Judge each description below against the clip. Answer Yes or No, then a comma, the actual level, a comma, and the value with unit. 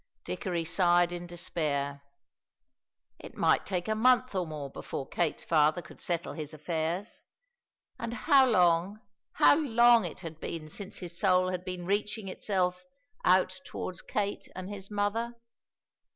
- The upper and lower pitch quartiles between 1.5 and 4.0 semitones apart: Yes, average, 3.5 semitones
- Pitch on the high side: No, medium, 180 Hz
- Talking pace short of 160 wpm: Yes, average, 145 wpm